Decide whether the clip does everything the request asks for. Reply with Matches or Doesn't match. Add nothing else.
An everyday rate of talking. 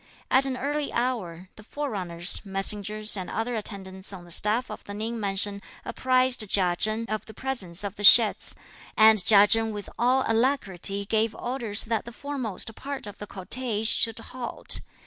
Matches